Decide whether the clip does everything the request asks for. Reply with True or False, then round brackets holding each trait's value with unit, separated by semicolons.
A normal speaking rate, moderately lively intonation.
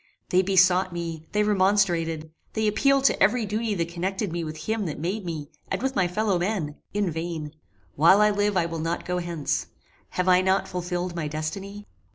True (195 wpm; 3.6 semitones)